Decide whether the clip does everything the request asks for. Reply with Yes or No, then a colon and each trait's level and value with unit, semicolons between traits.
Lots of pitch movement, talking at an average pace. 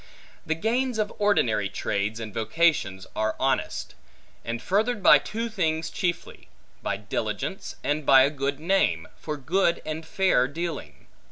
Yes: wide, 7.4 semitones; average, 145 wpm